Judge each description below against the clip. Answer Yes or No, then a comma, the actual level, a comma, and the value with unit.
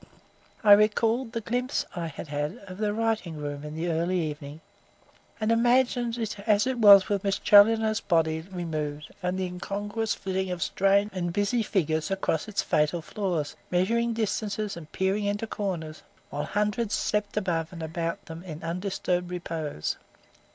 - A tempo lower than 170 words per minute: Yes, average, 160 wpm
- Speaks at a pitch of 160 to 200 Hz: Yes, high, 190 Hz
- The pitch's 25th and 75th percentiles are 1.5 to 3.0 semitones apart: No, average, 4.3 semitones